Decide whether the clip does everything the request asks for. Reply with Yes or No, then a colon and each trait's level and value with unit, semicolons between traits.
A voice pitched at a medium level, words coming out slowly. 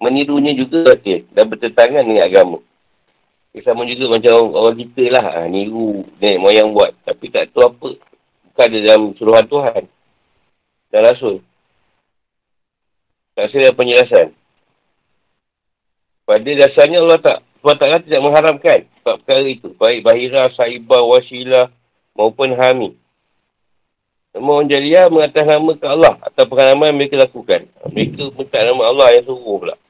No: medium, 155 Hz; average, 145 wpm